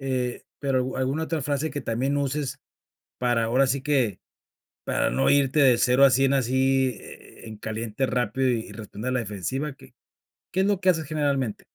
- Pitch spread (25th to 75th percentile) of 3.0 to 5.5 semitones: No, narrow, 2.5 semitones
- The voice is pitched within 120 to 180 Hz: Yes, low, 130 Hz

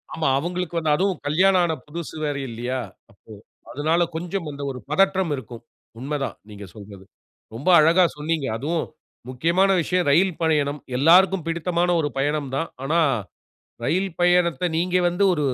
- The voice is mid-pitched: Yes, medium, 160 Hz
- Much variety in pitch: No, average, 3.8 semitones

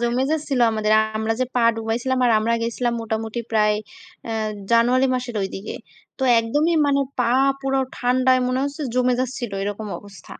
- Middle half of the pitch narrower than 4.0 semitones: Yes, narrow, 2.6 semitones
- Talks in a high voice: Yes, high, 240 Hz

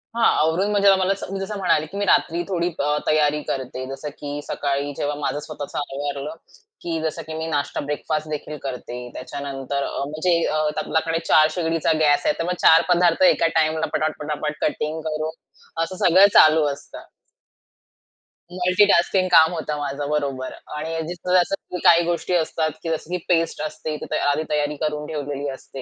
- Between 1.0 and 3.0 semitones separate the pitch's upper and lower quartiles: Yes, average, 2.7 semitones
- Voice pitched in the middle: Yes, medium, 155 Hz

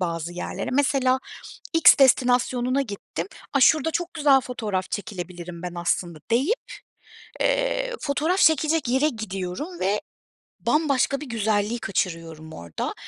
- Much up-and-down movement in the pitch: Yes, wide, 8.1 semitones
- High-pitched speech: Yes, high, 245 Hz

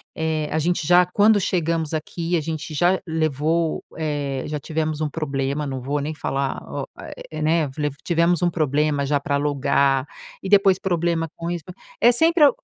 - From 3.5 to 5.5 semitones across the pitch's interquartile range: No, average, 2.8 semitones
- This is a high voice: No, medium, 155 Hz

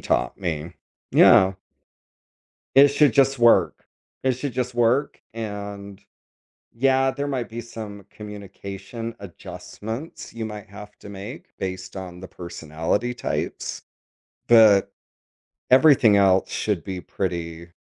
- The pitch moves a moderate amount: Yes, average, 4.4 semitones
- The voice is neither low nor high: No, low, 105 Hz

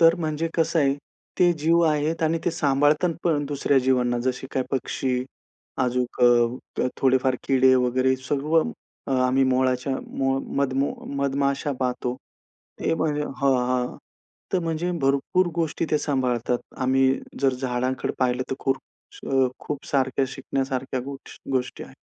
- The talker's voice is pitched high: No, low, 135 Hz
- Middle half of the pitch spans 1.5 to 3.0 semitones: Yes, narrow, 2.5 semitones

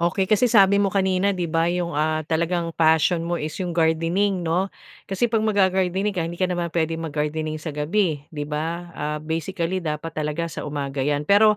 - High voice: No, medium, 170 Hz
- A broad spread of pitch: No, average, 3.3 semitones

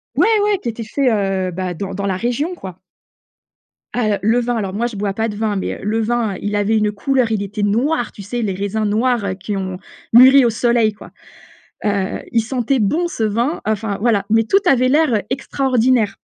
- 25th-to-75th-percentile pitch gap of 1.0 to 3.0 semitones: No, average, 3.4 semitones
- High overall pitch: Yes, high, 220 Hz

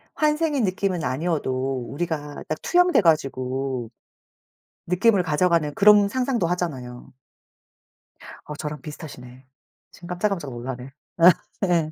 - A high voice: No, medium, 160 Hz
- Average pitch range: No, wide, 5.8 semitones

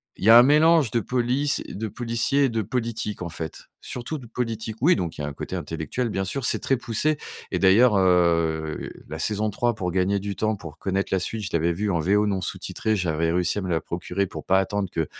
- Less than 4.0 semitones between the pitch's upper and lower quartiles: No, average, 4.8 semitones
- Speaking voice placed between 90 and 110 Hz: Yes, low, 100 Hz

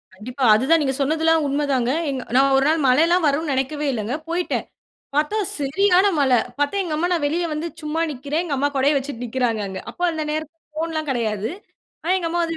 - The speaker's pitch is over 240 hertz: Yes, very high, 290 Hz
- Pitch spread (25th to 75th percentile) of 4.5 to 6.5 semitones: No, average, 3.7 semitones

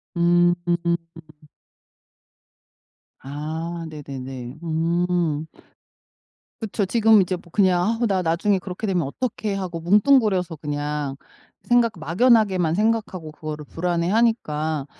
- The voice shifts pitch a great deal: No, average, 4.6 semitones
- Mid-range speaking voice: Yes, medium, 175 Hz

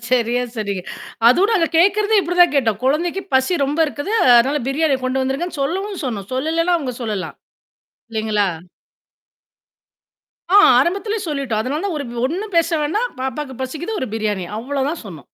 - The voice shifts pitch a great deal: Yes, wide, 5.9 semitones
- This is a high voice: Yes, very high, 280 Hz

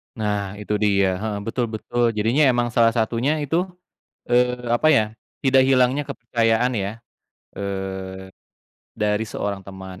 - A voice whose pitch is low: Yes, low, 110 Hz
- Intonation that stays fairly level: No, average, 3.6 semitones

